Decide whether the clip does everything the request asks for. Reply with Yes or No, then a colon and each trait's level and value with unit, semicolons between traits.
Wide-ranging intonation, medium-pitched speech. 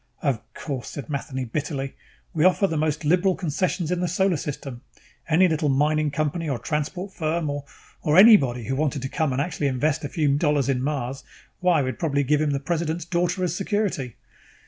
No: average, 3.7 semitones; medium, 150 Hz